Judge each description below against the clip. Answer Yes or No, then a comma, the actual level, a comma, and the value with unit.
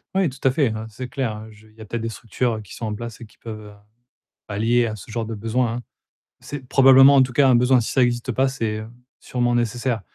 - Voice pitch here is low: Yes, low, 120 Hz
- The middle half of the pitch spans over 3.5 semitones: No, average, 2.8 semitones